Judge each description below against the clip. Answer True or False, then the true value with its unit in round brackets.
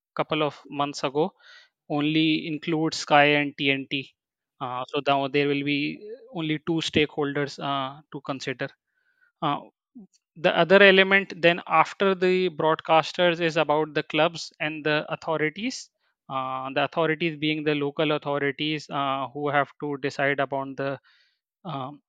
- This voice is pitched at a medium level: True (155 Hz)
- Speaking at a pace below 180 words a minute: True (140 wpm)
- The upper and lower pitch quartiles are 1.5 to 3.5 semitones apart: True (2.6 semitones)